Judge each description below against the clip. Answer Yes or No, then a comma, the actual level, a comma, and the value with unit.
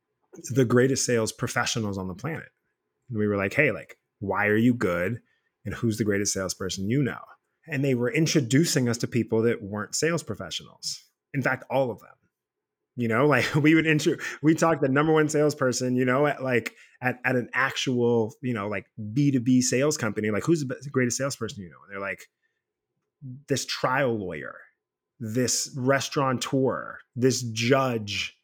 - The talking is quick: No, average, 185 wpm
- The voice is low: Yes, low, 125 Hz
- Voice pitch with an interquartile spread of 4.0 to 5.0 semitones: Yes, average, 4.3 semitones